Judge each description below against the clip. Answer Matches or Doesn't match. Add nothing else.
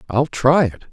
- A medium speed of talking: Matches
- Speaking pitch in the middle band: Doesn't match